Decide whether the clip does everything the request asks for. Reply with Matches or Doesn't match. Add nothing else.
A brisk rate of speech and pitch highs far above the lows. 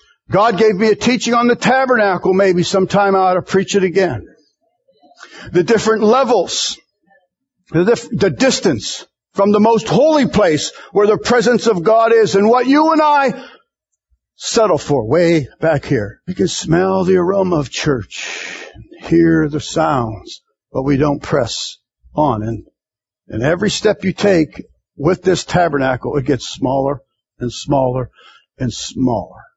Doesn't match